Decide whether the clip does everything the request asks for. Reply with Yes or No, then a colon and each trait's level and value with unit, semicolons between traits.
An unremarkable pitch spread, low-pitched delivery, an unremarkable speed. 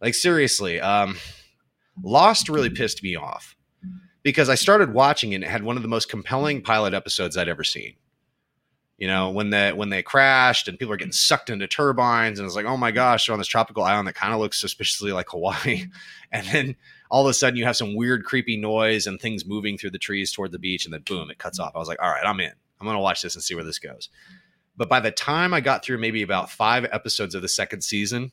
No: average, 5.0 semitones; low, 120 Hz; fast, 250 wpm